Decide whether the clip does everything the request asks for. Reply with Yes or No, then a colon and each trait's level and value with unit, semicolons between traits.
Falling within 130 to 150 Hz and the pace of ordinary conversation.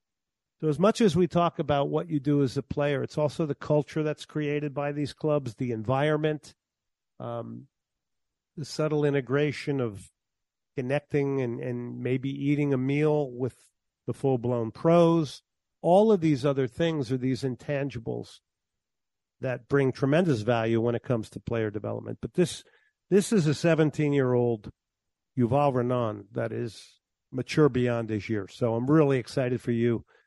Yes: medium, 140 Hz; average, 160 wpm